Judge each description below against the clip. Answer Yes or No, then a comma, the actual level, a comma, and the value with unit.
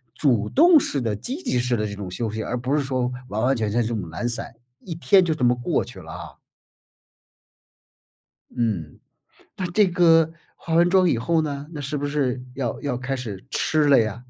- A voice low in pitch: Yes, low, 130 Hz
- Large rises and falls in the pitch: Yes, wide, 5.9 semitones